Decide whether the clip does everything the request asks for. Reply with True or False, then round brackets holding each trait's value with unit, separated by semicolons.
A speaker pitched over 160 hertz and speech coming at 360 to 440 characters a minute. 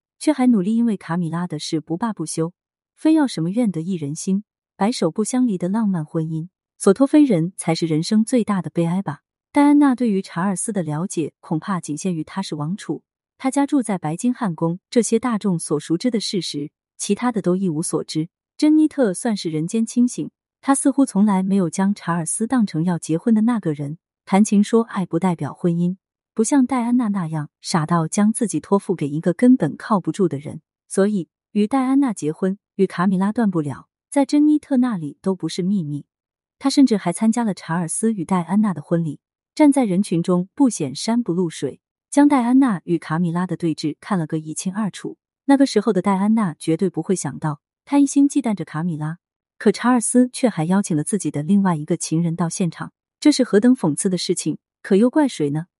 False (190 Hz; 310 characters per minute)